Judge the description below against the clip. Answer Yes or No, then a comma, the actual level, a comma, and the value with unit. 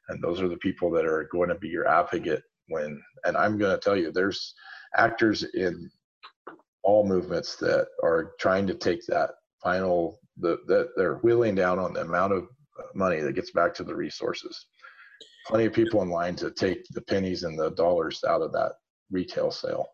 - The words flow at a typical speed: Yes, average, 195 wpm